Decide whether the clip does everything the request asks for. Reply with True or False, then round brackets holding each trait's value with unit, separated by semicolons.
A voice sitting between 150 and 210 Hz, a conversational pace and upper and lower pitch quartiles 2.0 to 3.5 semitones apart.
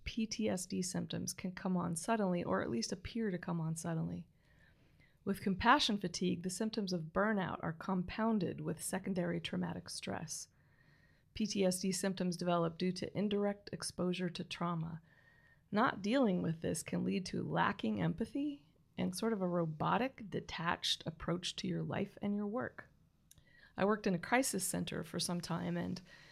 True (185 Hz; 155 wpm; 3.0 semitones)